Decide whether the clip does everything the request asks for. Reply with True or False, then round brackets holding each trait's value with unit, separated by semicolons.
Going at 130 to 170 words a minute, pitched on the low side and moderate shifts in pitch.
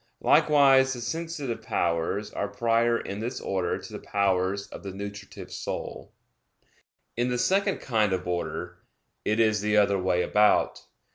True (150 wpm; 105 Hz; 4.0 semitones)